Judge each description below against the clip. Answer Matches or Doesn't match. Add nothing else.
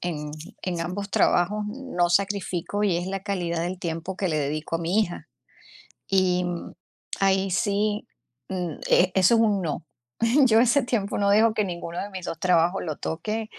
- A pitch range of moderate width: Matches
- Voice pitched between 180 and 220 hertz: Matches